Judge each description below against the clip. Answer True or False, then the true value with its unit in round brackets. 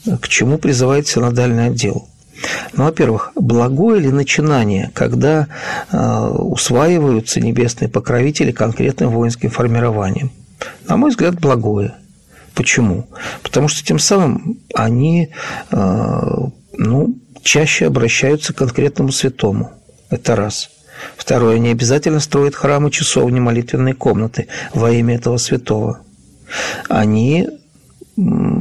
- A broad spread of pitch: False (4.6 semitones)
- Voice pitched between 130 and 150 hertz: True (135 Hz)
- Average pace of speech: False (105 wpm)